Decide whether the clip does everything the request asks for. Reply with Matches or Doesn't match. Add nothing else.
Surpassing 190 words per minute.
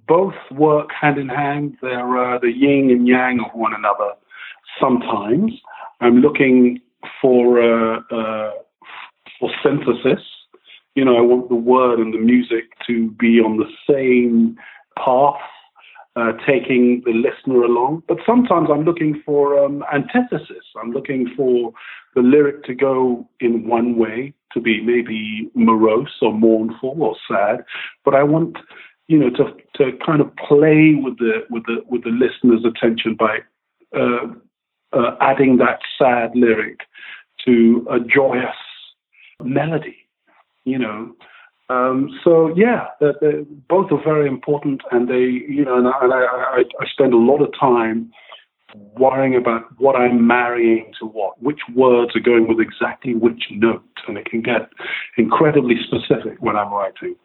Doesn't match